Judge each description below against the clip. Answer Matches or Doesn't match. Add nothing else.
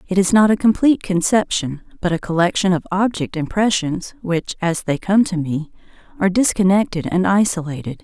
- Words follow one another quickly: Doesn't match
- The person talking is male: Doesn't match